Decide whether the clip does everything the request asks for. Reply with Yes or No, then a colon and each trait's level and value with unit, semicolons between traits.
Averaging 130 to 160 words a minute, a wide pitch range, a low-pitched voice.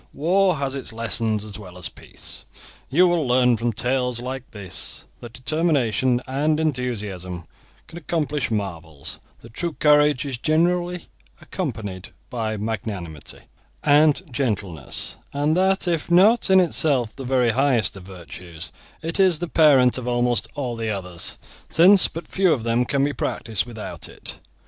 Yes: average, 150 wpm; wide, 6.1 semitones; low, 125 Hz